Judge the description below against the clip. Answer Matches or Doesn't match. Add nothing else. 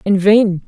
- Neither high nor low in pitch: Doesn't match